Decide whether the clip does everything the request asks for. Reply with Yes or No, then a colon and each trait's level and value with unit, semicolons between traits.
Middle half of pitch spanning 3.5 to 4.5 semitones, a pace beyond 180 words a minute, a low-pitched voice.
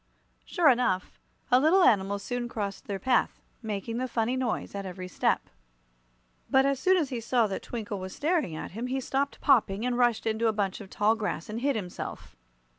No: average, 4.2 semitones; average, 195 wpm; high, 230 Hz